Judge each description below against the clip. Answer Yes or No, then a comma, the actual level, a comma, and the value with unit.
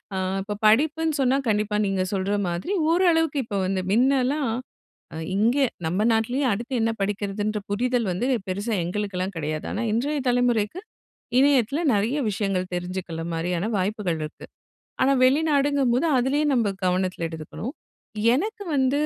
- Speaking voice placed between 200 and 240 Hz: Yes, high, 220 Hz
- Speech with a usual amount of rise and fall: No, wide, 6.2 semitones